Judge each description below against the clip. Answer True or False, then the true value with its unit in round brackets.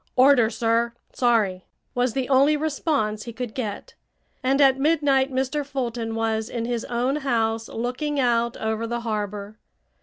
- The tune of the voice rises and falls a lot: False (3.1 semitones)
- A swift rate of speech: False (150 wpm)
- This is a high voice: True (240 Hz)